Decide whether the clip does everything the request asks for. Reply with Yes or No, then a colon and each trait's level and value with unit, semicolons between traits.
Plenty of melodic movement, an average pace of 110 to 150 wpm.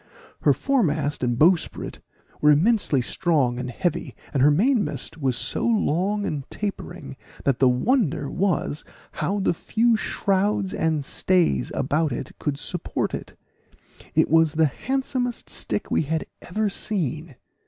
Yes: wide, 6.1 semitones; average, 140 wpm